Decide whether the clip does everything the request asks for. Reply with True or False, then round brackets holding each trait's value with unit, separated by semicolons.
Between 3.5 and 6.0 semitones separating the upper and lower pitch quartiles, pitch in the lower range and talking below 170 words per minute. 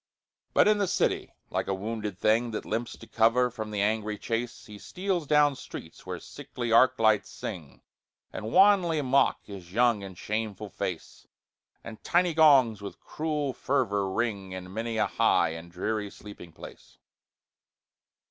True (4.3 semitones; 110 Hz; 155 wpm)